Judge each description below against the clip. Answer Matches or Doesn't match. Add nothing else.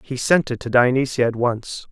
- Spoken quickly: Matches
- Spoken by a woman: Doesn't match